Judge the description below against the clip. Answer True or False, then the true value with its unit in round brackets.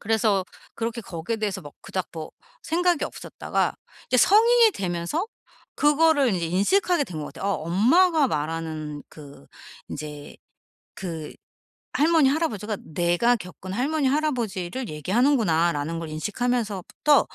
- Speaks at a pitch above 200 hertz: True (210 Hz)